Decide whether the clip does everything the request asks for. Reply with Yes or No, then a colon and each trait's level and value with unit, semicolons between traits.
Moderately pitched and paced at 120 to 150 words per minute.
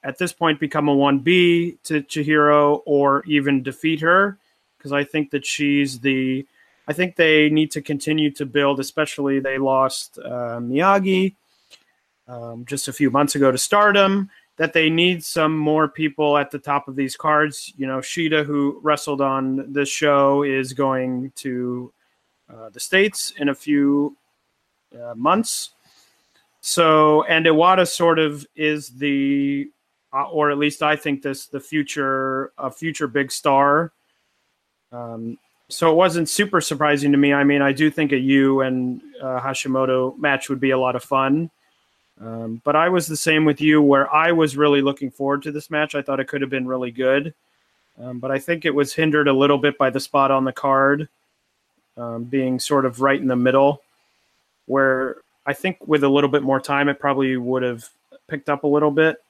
No: medium, 145 Hz; average, 185 wpm